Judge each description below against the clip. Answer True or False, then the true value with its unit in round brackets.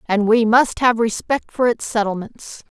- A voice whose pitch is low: False (225 Hz)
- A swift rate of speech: False (175 wpm)